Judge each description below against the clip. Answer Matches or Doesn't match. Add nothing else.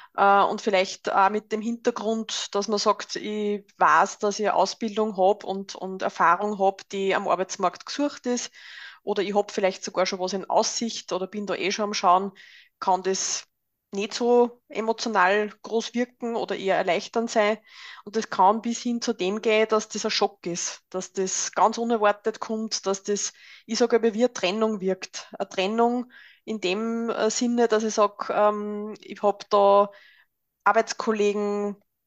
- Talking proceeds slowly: Doesn't match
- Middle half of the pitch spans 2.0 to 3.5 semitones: Matches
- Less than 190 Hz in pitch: Doesn't match